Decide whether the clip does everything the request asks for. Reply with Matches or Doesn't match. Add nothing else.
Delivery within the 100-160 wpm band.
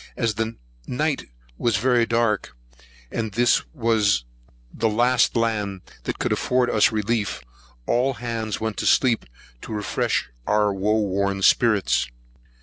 Matches